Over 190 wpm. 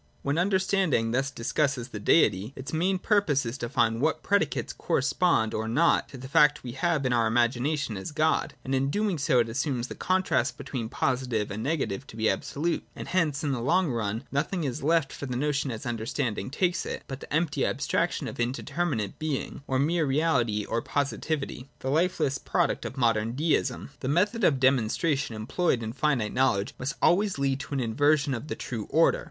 Yes: average, 200 wpm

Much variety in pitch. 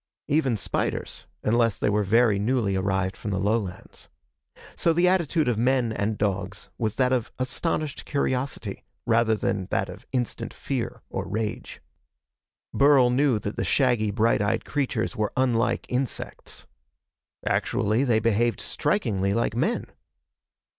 No: average, 3.9 semitones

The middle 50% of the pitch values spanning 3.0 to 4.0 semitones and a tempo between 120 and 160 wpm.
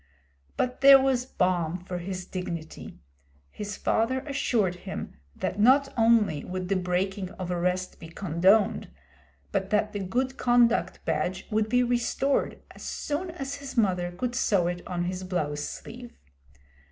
No: wide, 5.4 semitones; average, 150 wpm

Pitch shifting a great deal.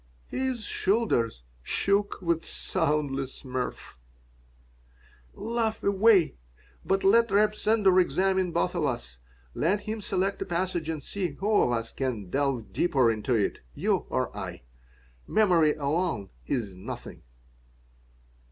Yes: wide, 7.3 semitones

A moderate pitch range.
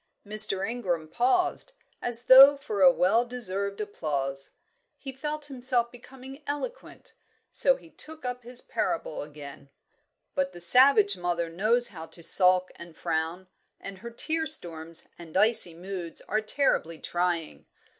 No: wide, 7.0 semitones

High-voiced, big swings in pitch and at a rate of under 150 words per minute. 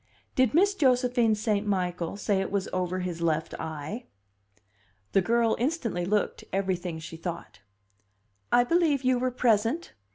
Yes: high, 210 Hz; wide, 5.7 semitones; average, 140 wpm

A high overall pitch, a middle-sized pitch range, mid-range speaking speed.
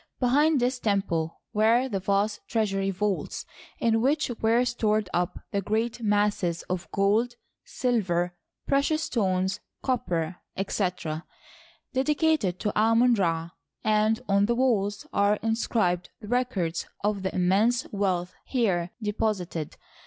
No: high, 210 Hz; average, 4.2 semitones; slow, 125 wpm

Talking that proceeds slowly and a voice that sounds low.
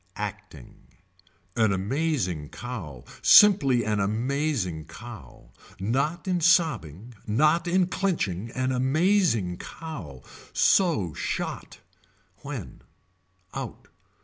Yes: slow, 90 wpm; low, 120 Hz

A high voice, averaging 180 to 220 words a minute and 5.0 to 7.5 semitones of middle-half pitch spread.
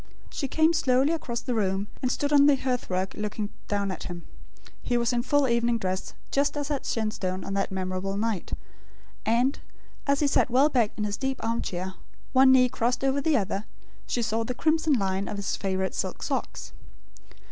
Yes: high, 235 Hz; average, 195 wpm; wide, 5.4 semitones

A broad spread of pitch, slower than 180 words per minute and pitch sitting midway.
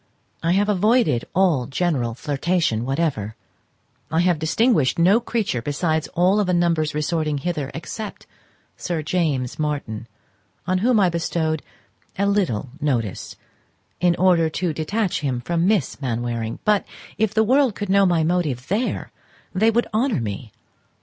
Yes: wide, 5.7 semitones; average, 145 wpm; medium, 170 Hz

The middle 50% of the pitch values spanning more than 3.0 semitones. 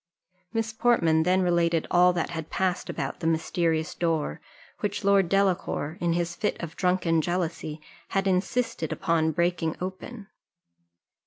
No: narrow, 2.5 semitones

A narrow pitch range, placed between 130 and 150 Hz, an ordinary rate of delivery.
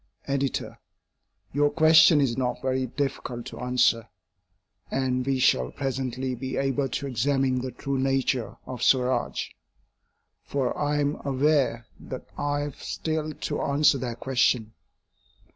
No: narrow, 2.2 semitones; low, 135 Hz; slow, 130 wpm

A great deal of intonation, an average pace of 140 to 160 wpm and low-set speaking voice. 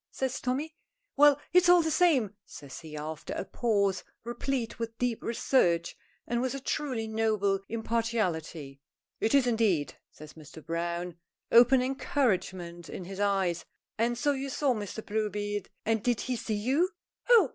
No: wide, 5.7 semitones; average, 155 wpm; high, 225 Hz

